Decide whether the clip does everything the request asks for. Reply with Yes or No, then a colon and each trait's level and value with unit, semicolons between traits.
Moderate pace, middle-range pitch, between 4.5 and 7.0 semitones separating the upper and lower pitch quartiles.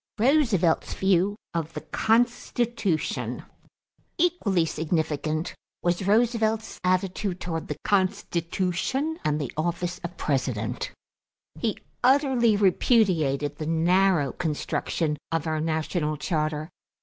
No: slow, 100 wpm; medium, 175 Hz; wide, 5.4 semitones